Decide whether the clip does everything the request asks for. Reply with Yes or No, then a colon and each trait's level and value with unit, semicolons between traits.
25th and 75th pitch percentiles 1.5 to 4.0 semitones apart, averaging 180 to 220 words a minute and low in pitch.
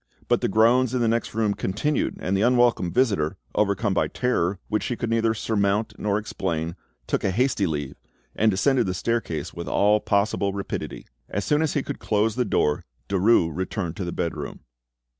Yes: average, 3.7 semitones; average, 185 wpm; low, 105 Hz